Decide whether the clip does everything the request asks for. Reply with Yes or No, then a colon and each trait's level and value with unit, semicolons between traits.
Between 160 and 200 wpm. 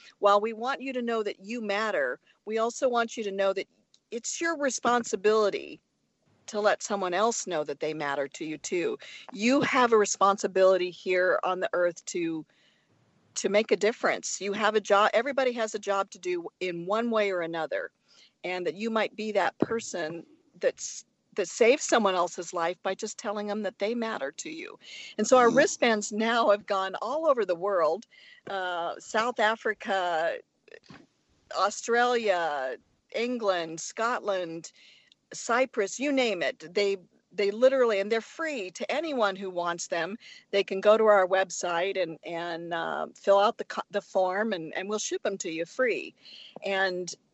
Yes: average, 170 wpm